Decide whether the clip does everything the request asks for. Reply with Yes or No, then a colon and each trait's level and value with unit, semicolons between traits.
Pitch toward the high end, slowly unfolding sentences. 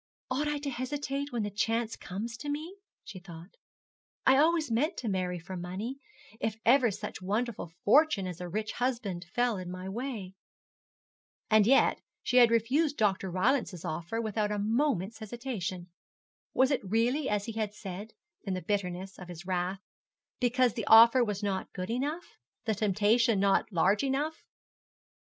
No: high, 220 Hz; average, 165 wpm